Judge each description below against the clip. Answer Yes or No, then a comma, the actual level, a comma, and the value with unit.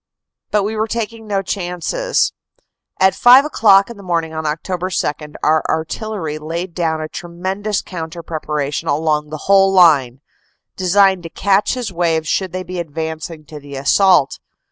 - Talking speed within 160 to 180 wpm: Yes, average, 165 wpm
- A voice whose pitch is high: No, medium, 175 Hz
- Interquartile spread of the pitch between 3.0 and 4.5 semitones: Yes, average, 3.8 semitones